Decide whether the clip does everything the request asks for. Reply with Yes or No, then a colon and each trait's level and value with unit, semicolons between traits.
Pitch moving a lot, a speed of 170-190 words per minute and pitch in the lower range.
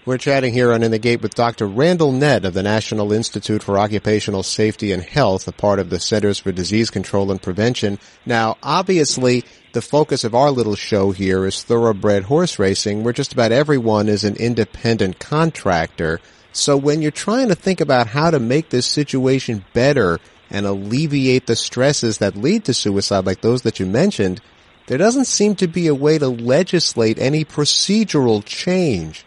Yes: wide, 5.8 semitones; average, 180 wpm; low, 115 Hz